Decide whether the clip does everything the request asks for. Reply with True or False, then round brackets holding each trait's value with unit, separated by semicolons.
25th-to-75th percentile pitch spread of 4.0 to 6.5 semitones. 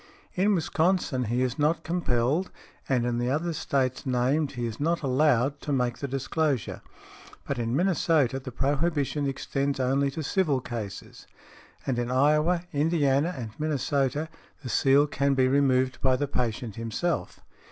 False (3.2 semitones)